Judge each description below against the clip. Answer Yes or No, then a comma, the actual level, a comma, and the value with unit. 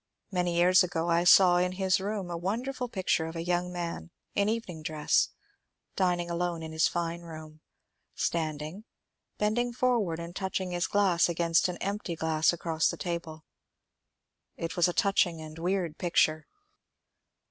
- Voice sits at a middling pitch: Yes, medium, 175 Hz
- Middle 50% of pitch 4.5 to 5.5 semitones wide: No, narrow, 2.4 semitones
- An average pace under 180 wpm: Yes, average, 160 wpm